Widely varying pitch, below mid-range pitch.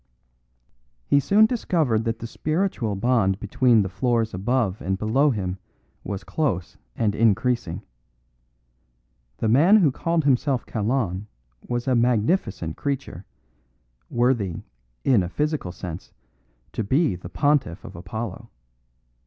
Yes: wide, 5.9 semitones; low, 115 Hz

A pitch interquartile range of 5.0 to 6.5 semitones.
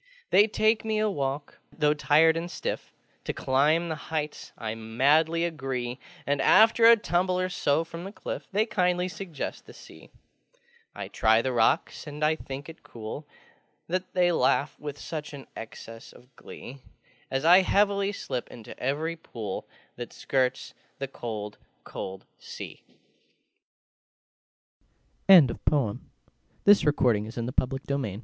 Yes: average, 5.3 semitones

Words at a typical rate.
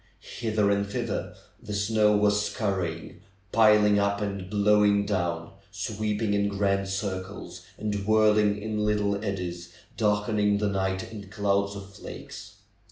No: slow, 130 wpm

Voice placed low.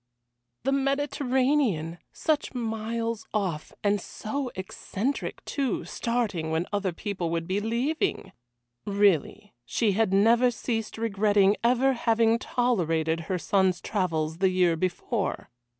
No: high, 210 Hz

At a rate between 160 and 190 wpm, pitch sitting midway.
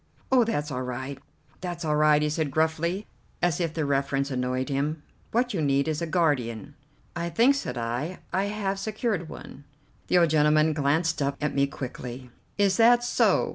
Yes: average, 180 wpm; medium, 155 Hz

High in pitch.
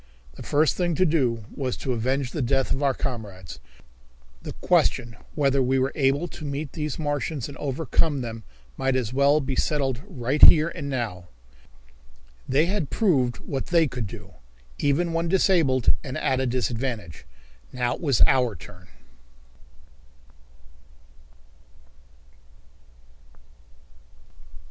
No: low, 135 Hz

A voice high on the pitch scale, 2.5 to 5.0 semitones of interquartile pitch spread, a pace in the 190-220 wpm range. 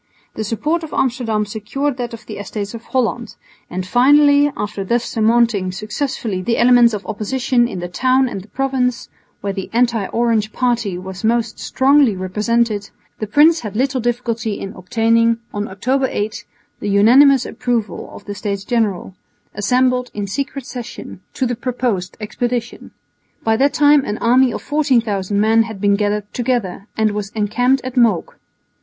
No: high, 230 Hz; average, 3.4 semitones; average, 160 wpm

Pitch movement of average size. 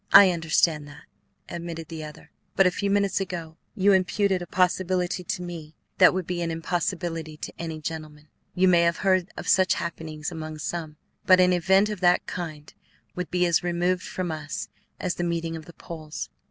No: narrow, 2.2 semitones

